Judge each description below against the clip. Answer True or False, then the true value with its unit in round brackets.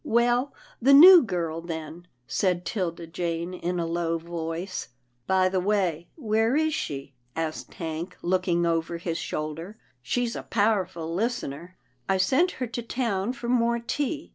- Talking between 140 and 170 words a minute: False (180 wpm)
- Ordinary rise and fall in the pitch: False (5.9 semitones)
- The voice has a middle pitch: True (180 Hz)